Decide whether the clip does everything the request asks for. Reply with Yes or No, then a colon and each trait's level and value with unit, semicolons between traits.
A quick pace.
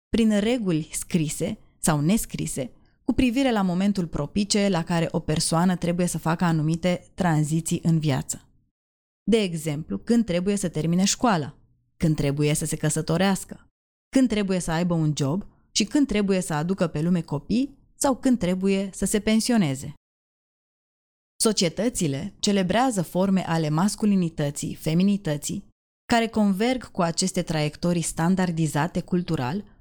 No: average, 135 wpm